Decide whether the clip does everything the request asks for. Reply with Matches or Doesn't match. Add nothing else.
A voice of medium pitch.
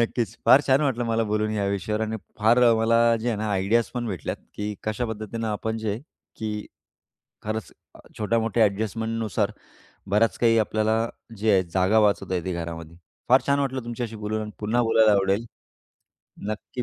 Doesn't match